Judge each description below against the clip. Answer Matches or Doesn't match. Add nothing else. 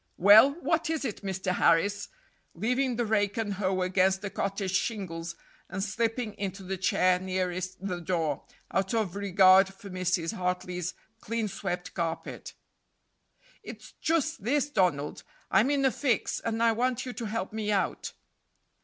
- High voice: Matches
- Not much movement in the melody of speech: Doesn't match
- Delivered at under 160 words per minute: Matches